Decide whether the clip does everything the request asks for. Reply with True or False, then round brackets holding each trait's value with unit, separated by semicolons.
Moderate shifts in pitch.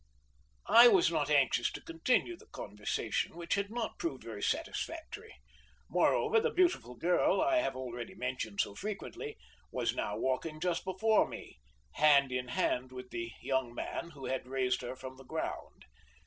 False (8.5 semitones)